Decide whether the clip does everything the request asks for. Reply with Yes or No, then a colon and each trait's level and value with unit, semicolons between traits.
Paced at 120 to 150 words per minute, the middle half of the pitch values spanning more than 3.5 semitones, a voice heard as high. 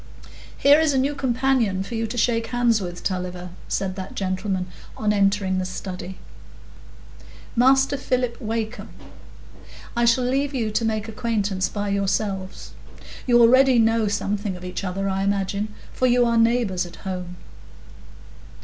Yes: average, 145 wpm; average, 4.1 semitones; high, 215 Hz